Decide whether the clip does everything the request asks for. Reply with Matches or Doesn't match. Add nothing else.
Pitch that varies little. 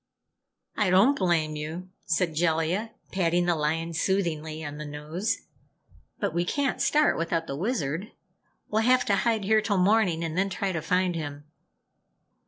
Doesn't match